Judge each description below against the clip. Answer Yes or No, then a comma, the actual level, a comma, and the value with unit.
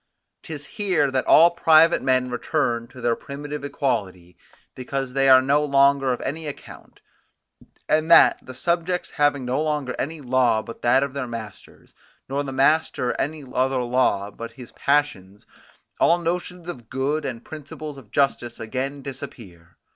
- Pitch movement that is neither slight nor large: Yes, average, 3.2 semitones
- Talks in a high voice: No, low, 135 Hz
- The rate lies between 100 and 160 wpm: Yes, average, 155 wpm